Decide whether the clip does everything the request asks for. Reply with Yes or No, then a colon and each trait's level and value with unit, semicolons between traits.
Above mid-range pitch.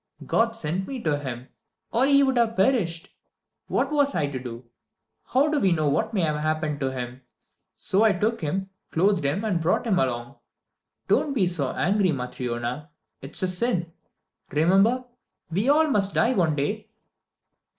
No: medium, 180 Hz